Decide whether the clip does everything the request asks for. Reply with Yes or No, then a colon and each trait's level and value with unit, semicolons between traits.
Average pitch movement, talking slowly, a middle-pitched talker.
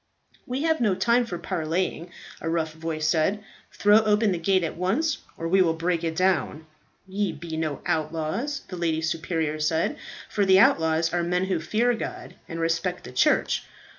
No: average, 3.5 semitones; average, 180 wpm; medium, 175 Hz